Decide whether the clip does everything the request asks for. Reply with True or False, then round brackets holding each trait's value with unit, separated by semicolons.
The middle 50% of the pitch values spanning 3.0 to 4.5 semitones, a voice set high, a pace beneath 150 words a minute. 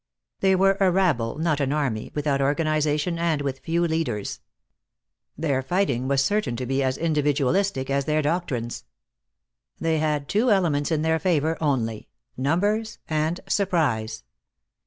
False (3.9 semitones; 150 Hz; 140 wpm)